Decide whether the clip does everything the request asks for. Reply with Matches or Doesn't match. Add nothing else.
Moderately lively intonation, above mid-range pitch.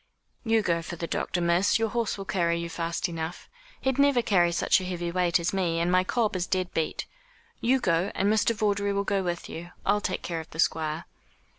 Doesn't match